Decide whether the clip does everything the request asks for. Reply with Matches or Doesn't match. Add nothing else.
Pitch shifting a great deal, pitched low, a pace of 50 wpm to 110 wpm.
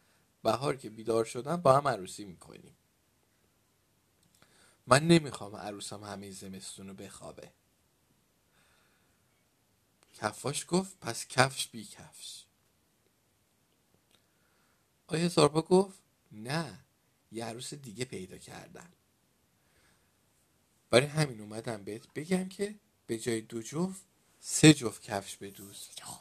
Matches